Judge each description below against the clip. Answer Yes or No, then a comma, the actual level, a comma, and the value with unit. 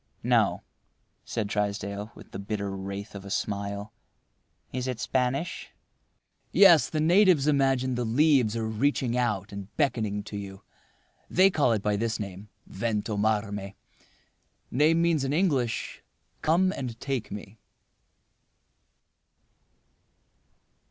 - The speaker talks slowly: Yes, slow, 110 wpm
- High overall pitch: No, low, 115 Hz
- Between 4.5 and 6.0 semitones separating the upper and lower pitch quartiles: Yes, average, 5.2 semitones